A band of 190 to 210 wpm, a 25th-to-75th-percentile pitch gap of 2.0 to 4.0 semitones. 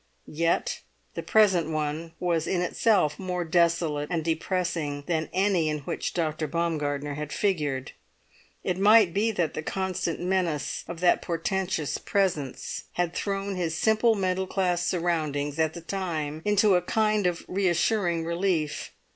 No: average, 145 wpm; average, 3.3 semitones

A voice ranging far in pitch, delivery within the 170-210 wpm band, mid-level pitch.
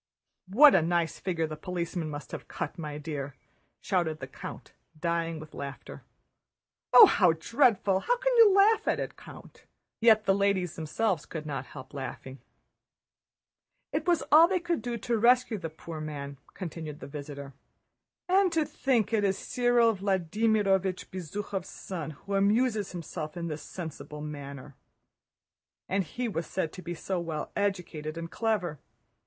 No: wide, 6.1 semitones; average, 155 wpm; medium, 180 Hz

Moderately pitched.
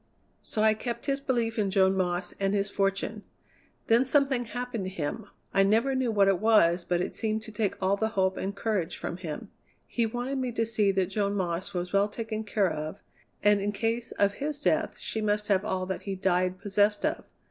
No: high, 205 Hz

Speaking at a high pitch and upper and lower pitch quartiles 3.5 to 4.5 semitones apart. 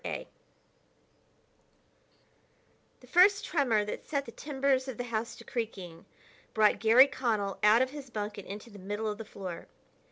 Yes: high, 225 Hz; average, 4.2 semitones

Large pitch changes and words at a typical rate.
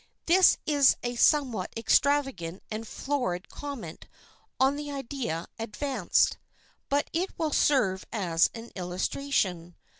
No: wide, 7.4 semitones; slow, 115 wpm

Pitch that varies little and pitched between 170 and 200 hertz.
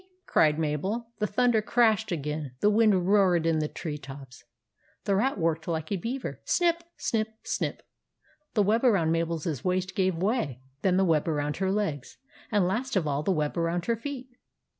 No: wide, 5.4 semitones; medium, 185 Hz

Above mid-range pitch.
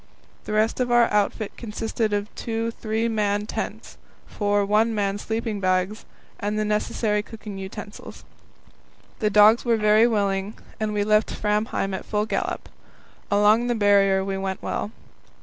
Yes: high, 210 Hz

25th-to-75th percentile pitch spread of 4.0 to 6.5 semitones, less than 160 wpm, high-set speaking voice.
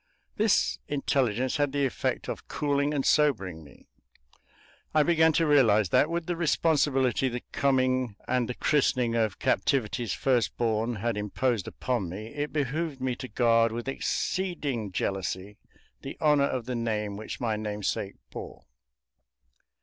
No: average, 4.8 semitones; average, 145 wpm; low, 125 Hz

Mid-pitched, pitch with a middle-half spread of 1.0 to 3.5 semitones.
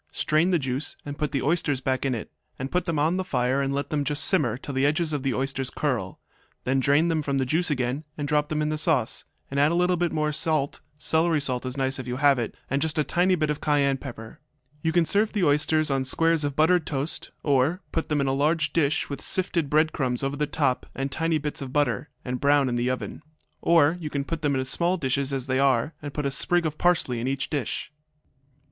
Yes: medium, 145 Hz; average, 3.0 semitones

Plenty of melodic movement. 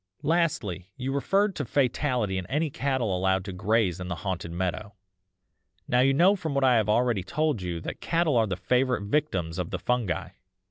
Yes: wide, 7.1 semitones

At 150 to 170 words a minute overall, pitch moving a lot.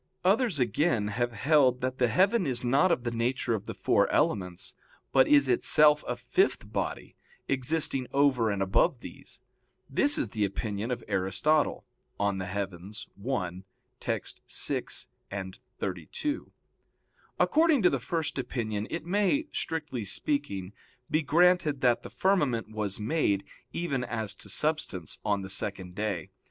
No: average, 140 wpm; wide, 6.9 semitones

